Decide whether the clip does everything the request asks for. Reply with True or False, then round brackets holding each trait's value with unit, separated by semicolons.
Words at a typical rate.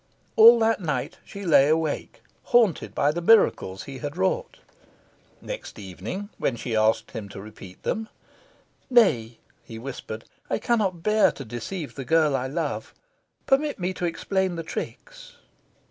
True (155 wpm)